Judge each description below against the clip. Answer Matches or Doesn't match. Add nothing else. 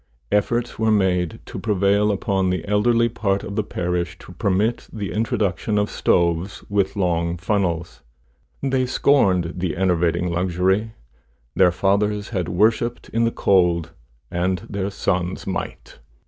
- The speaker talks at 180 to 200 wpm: Doesn't match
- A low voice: Matches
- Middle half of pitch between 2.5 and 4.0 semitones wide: Matches